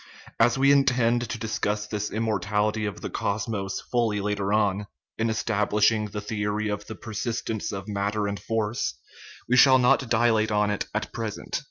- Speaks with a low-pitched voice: Yes, low, 105 Hz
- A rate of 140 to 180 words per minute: Yes, average, 170 wpm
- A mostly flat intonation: Yes, narrow, 1.7 semitones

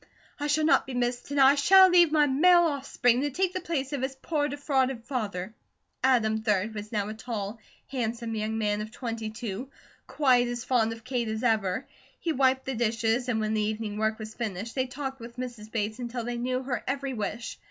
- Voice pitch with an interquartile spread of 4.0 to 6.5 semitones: No, average, 3.6 semitones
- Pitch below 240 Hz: No, high, 245 Hz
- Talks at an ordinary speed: No, fast, 210 wpm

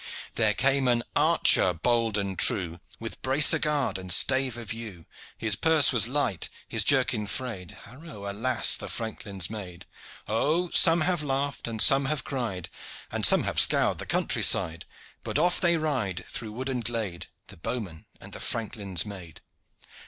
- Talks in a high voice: No, low, 115 Hz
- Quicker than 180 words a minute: No, average, 165 wpm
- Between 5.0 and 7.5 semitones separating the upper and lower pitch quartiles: Yes, wide, 5.4 semitones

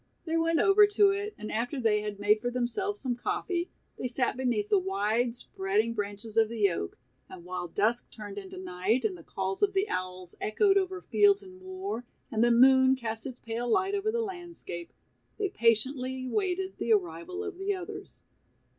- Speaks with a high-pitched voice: Yes, high, 245 Hz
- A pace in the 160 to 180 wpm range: No, average, 190 wpm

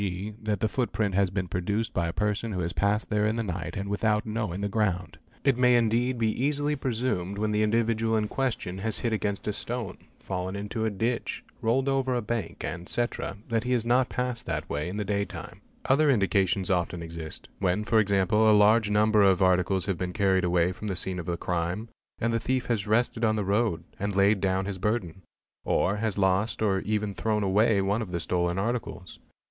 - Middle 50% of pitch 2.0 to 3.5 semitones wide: Yes, average, 3.2 semitones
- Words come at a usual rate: No, fast, 215 wpm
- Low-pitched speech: Yes, low, 105 Hz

